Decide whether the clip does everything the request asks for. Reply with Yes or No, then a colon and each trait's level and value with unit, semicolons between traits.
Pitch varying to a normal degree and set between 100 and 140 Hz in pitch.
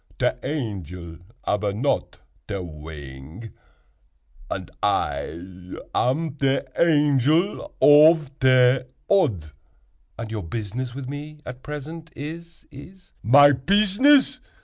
No: wide, 7.4 semitones; low, 135 Hz